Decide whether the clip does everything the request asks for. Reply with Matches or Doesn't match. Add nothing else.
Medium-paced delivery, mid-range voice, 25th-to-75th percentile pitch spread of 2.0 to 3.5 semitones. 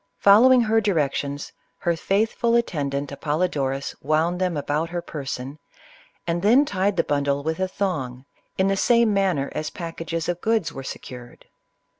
Doesn't match